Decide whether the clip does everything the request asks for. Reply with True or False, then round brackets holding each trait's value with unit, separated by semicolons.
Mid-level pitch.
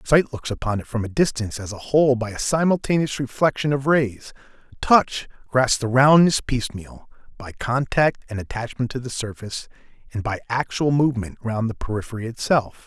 False (125 Hz)